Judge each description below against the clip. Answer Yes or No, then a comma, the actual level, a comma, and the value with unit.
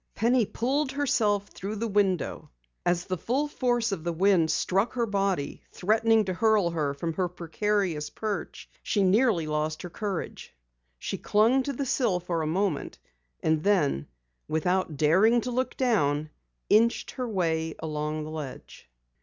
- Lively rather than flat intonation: Yes, wide, 5.8 semitones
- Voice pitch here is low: No, high, 195 Hz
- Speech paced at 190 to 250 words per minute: No, average, 155 wpm